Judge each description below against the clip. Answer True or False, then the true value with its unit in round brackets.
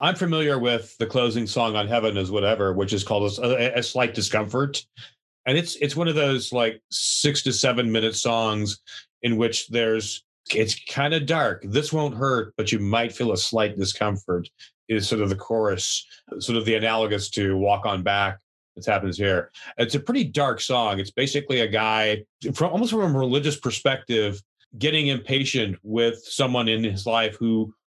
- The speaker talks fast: False (185 wpm)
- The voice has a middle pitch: False (115 Hz)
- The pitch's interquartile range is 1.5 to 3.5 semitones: False (4.0 semitones)